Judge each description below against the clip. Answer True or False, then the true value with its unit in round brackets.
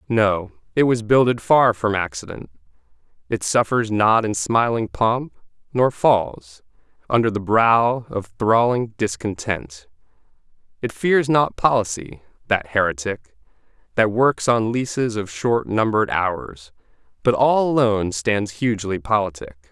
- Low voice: True (110 Hz)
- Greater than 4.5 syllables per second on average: False (4.2 syllables/s)